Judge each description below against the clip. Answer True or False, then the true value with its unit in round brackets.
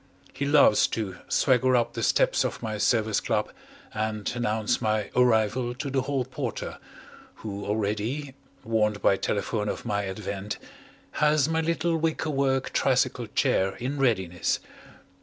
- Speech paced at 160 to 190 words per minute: False (140 wpm)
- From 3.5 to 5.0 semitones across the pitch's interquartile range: True (4.5 semitones)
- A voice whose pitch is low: True (115 Hz)